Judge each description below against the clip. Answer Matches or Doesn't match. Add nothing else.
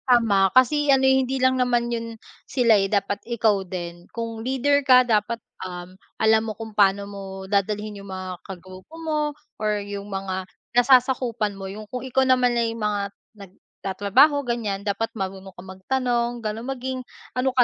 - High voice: Matches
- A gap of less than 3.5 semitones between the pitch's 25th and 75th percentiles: Doesn't match